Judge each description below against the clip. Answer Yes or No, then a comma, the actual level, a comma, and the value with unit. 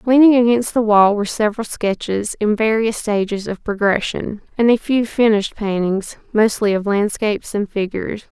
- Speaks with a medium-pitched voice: No, high, 215 Hz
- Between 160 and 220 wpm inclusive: No, average, 150 wpm